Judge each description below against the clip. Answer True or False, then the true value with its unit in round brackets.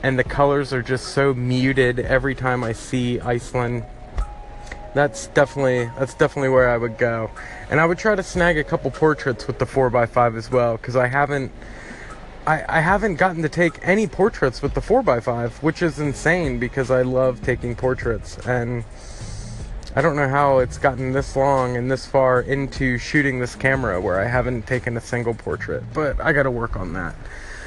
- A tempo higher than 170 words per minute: True (185 wpm)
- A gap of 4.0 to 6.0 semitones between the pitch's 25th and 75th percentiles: False (2.8 semitones)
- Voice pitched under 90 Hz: False (130 Hz)